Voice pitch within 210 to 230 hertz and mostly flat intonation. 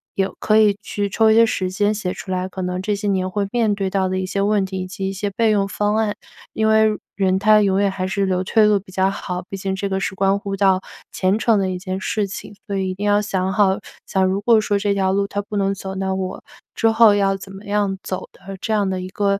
No: high, 195 Hz; narrow, 1.5 semitones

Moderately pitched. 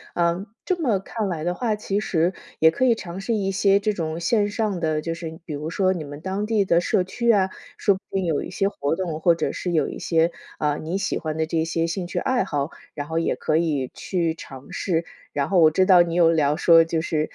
Yes: medium, 170 Hz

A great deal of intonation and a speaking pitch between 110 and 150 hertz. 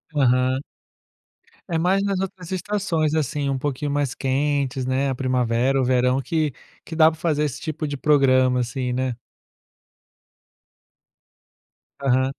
No: average, 3.3 semitones; medium, 140 Hz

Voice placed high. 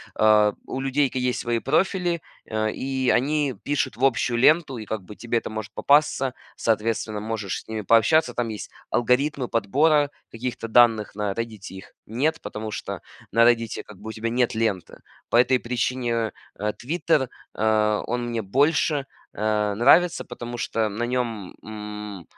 No: low, 115 Hz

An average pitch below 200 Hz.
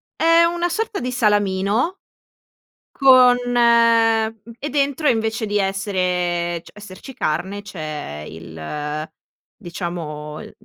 No: high, 205 Hz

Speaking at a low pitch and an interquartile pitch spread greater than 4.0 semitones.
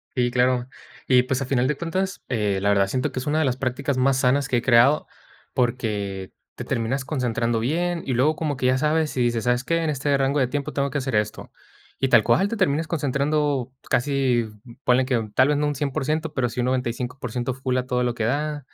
No: low, 130 Hz; average, 2.9 semitones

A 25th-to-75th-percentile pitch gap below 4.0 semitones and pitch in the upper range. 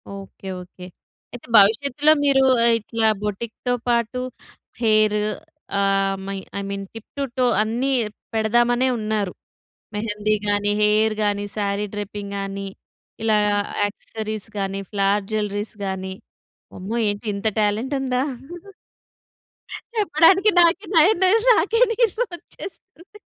No: average, 4.4 semitones; high, 215 Hz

